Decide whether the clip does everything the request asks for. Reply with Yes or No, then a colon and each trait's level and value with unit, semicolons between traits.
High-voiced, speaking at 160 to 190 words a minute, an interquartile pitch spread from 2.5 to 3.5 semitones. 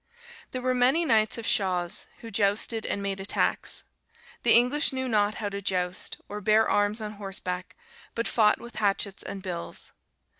Yes: high, 210 Hz; average, 165 wpm; average, 2.8 semitones